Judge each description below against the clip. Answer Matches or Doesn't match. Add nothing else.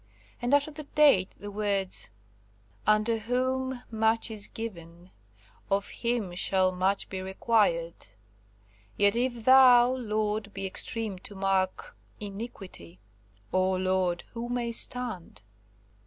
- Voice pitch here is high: Matches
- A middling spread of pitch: Matches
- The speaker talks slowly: Matches